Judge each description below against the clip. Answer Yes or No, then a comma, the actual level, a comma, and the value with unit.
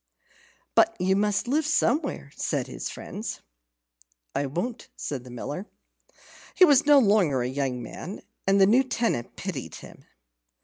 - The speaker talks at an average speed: Yes, average, 145 wpm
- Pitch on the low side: No, high, 195 Hz